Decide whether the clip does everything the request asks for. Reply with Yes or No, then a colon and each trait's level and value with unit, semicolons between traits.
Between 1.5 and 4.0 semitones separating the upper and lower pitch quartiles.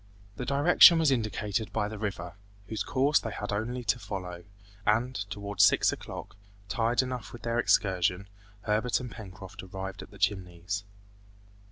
Yes: average, 3.6 semitones